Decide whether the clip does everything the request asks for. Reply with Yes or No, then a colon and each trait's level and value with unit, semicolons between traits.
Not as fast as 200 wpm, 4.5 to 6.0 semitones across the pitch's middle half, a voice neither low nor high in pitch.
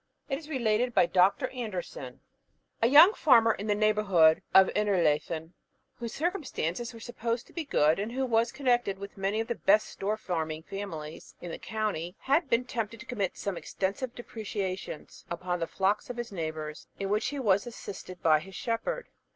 No: average, 180 wpm; average, 4.9 semitones; high, 210 Hz